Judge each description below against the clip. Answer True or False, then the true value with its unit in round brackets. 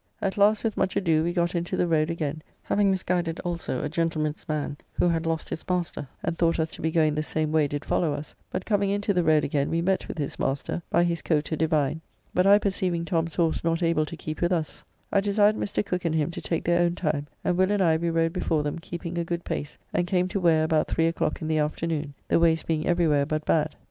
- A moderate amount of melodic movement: False (2.3 semitones)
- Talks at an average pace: False (255 wpm)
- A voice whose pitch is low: False (165 Hz)